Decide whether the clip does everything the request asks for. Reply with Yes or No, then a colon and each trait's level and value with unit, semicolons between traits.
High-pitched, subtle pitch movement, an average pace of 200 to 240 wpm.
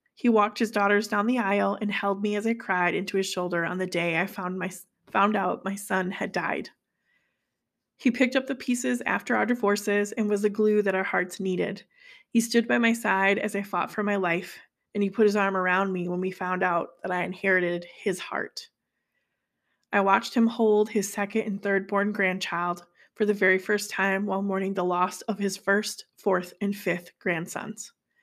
Yes: high, 200 Hz; narrow, 2.3 semitones; fast, 205 wpm